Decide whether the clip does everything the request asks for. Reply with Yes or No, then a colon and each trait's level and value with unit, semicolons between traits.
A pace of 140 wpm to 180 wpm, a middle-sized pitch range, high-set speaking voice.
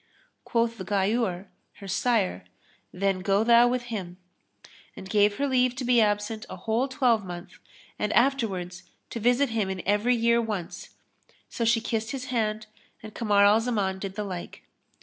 Yes: average, 160 wpm; average, 3.3 semitones; high, 215 Hz